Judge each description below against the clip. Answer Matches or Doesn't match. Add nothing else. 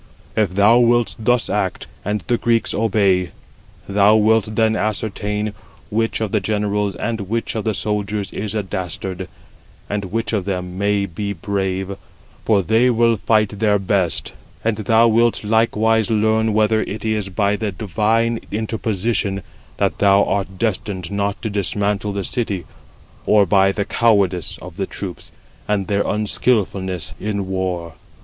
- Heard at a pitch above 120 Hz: Doesn't match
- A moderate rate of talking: Matches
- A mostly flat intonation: Matches